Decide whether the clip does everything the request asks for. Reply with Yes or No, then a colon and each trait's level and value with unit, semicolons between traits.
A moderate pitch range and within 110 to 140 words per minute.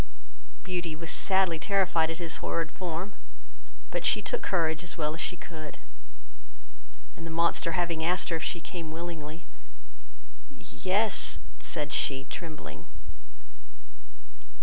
No: narrow, 2.0 semitones; slow, 135 wpm